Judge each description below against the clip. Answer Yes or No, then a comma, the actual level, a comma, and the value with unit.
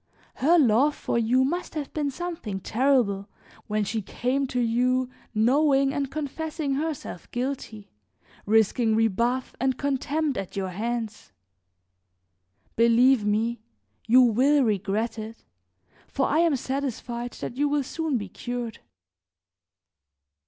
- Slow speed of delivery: Yes, slow, 125 wpm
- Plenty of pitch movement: No, average, 4.0 semitones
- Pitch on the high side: Yes, very high, 250 Hz